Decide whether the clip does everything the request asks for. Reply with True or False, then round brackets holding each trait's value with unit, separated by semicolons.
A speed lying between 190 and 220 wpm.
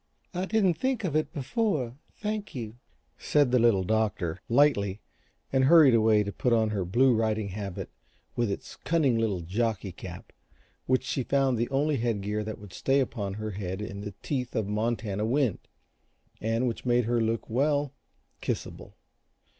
False (165 wpm)